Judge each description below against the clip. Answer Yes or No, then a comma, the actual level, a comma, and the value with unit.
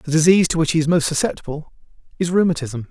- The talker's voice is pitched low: No, medium, 160 Hz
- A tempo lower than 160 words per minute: No, fast, 205 wpm